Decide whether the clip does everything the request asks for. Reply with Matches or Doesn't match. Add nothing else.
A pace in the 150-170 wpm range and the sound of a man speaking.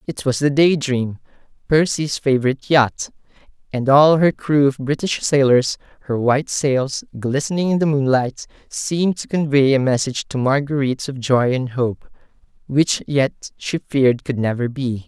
Matches